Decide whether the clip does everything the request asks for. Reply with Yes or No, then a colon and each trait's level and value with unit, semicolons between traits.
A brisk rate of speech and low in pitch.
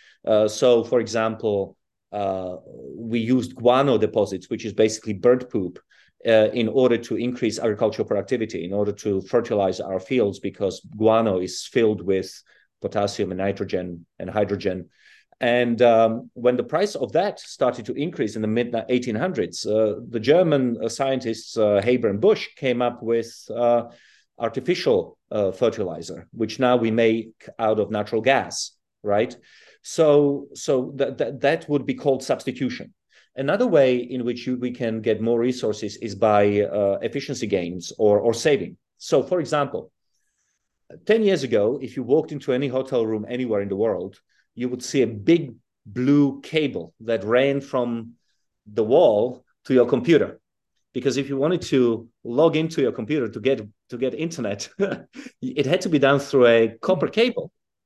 Yes: fast, 165 wpm; low, 120 Hz